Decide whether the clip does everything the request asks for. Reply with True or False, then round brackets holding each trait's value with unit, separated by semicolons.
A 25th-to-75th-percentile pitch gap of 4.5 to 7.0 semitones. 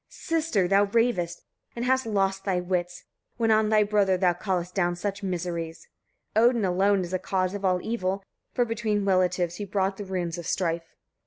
False (2.8 semitones)